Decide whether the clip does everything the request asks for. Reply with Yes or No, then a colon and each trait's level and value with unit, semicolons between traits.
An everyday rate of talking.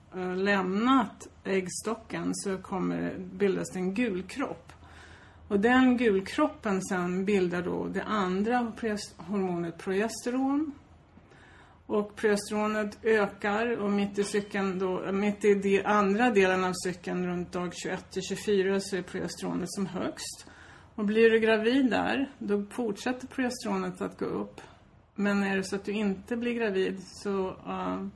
Yes: average, 145 wpm